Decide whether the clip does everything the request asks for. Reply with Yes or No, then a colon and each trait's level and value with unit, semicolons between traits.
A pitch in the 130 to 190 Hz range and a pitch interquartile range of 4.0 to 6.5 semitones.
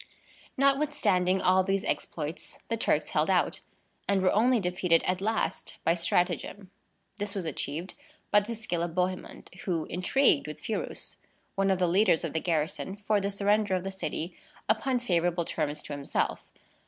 No: medium, 185 Hz; average, 3.1 semitones